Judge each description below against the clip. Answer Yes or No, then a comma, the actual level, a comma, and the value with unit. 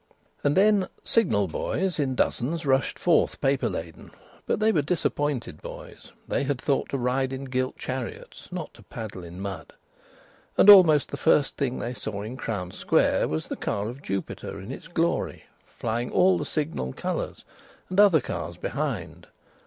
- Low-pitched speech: Yes, low, 130 Hz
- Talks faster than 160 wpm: Yes, average, 170 wpm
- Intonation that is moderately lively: No, wide, 6.6 semitones